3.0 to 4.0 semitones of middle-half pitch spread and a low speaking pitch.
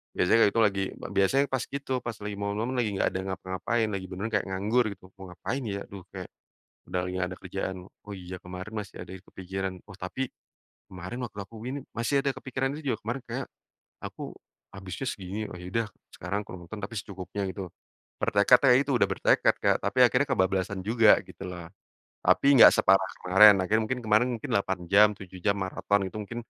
Yes: average, 3.6 semitones; low, 100 Hz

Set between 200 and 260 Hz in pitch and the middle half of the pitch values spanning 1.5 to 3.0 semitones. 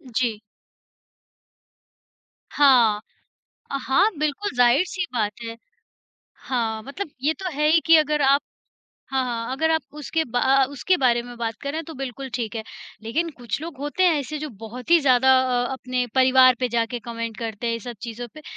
No: very high, 255 Hz; average, 4.1 semitones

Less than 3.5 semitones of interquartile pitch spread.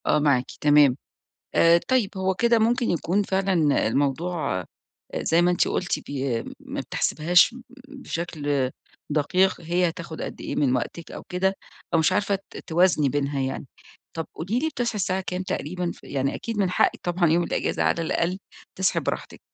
No: average, 4.3 semitones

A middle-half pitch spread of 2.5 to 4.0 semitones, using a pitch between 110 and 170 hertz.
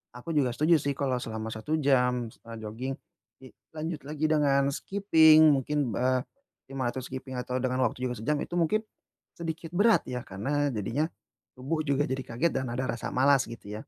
Yes: average, 3.7 semitones; low, 135 Hz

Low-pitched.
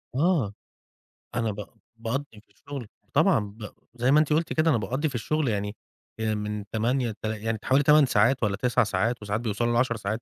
Yes: low, 115 Hz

